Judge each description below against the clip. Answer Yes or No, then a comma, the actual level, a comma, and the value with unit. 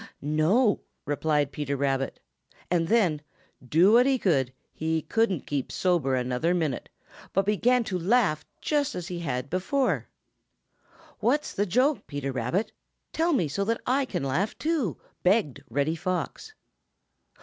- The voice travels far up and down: Yes, wide, 8.0 semitones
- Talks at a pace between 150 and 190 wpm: No, average, 140 wpm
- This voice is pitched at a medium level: Yes, medium, 175 Hz